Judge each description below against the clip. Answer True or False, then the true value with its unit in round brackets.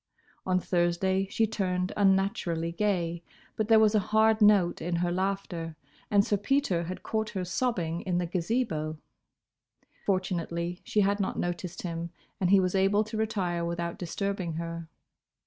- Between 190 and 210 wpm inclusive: False (155 wpm)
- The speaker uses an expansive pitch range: False (3.2 semitones)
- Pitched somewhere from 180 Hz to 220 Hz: True (185 Hz)